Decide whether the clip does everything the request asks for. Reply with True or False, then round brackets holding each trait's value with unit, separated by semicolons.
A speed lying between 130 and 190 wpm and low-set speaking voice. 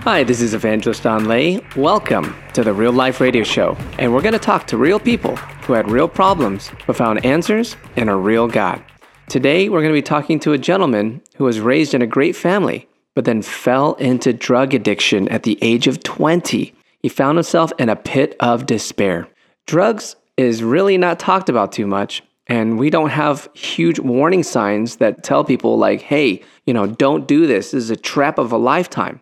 False (205 wpm; 130 Hz)